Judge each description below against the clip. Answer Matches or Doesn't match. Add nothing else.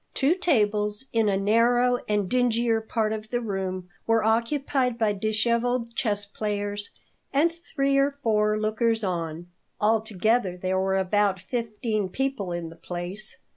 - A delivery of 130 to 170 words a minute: Matches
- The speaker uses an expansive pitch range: Doesn't match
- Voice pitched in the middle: Doesn't match